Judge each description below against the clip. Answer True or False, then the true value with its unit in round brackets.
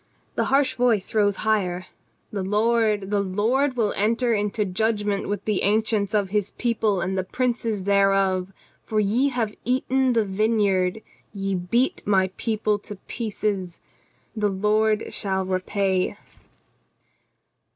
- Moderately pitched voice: False (210 Hz)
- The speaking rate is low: True (130 wpm)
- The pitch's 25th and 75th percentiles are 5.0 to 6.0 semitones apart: False (2.5 semitones)